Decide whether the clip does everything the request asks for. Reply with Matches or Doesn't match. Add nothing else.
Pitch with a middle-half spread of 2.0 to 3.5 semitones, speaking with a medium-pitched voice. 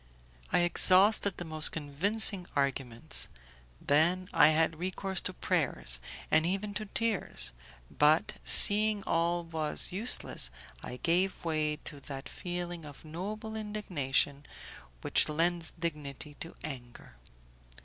Doesn't match